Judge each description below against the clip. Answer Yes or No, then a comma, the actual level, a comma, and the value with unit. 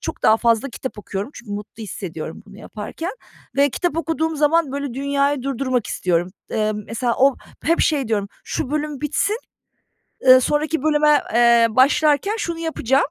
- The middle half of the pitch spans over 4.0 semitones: Yes, average, 4.9 semitones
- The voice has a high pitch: Yes, very high, 270 Hz